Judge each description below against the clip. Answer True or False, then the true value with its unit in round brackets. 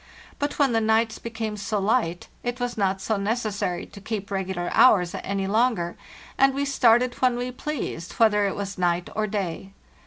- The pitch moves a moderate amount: True (3.9 semitones)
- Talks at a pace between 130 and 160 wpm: False (180 wpm)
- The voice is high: True (215 Hz)